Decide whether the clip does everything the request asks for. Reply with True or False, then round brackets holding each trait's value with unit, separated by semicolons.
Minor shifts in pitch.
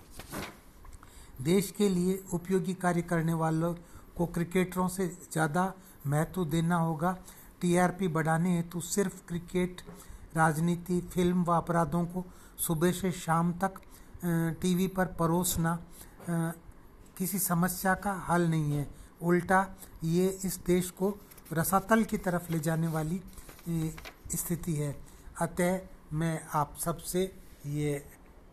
True (2.1 semitones)